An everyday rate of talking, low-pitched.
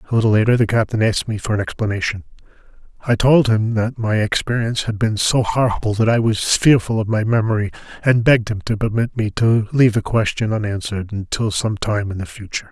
No: fast, 210 wpm; low, 110 Hz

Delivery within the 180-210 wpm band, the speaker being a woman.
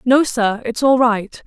Yes: fast, 205 wpm; female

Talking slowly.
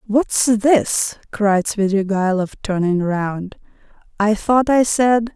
Yes: slow, 110 wpm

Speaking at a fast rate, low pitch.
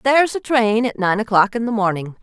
No: fast, 245 wpm; high, 220 Hz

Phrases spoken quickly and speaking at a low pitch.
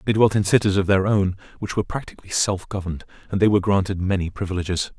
Yes: fast, 215 wpm; very low, 95 Hz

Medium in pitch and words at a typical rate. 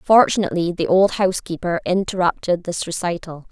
No: medium, 180 Hz; slow, 120 wpm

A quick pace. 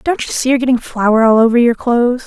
Yes: fast, 265 wpm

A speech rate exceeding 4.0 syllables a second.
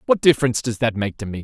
Yes: 8.0 syllables/s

